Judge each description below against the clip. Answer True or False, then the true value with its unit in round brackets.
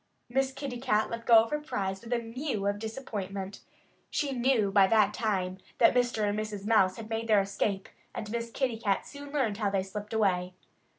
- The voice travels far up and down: False (3.3 semitones)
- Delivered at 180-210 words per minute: True (195 wpm)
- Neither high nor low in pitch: False (220 Hz)